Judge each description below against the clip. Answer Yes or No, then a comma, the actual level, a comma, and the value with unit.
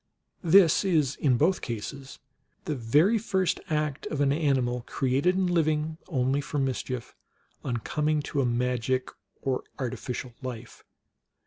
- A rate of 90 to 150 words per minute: Yes, average, 140 wpm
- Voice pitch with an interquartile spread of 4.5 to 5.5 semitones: No, average, 3.7 semitones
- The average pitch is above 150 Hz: No, medium, 140 Hz